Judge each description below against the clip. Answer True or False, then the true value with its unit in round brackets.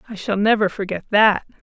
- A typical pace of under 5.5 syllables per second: True (5.3 syllables/s)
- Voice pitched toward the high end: True (205 Hz)